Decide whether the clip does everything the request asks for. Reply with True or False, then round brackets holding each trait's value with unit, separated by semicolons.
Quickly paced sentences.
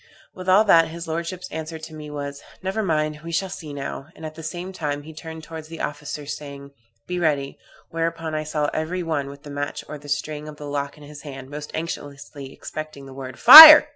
True (220 wpm)